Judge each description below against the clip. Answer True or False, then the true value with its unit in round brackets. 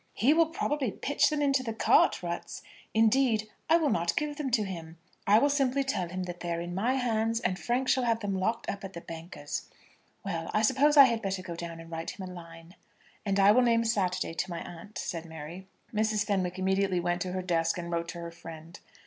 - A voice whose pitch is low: False (195 Hz)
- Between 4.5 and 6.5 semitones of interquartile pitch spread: True (5.6 semitones)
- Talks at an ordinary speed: False (230 wpm)